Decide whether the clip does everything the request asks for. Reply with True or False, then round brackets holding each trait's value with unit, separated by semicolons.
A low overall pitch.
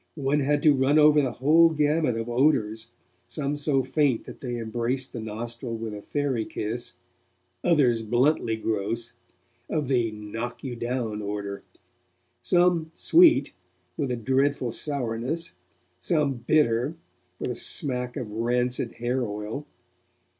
True (125 Hz)